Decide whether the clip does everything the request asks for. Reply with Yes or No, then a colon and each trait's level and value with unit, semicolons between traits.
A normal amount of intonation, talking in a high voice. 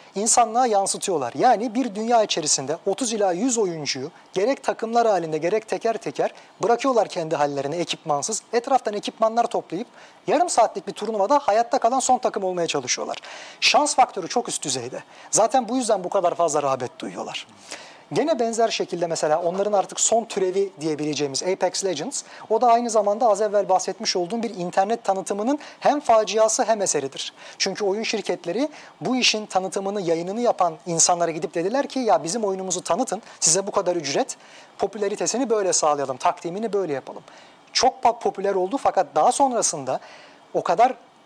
Yes: average, 4.5 semitones; high, 200 Hz